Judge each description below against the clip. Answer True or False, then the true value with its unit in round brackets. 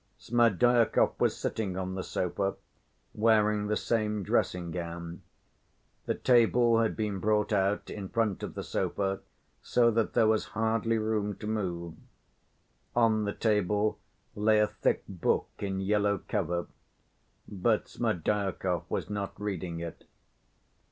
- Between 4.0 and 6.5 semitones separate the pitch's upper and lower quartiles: False (2.6 semitones)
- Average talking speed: False (130 wpm)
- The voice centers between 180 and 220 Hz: False (105 Hz)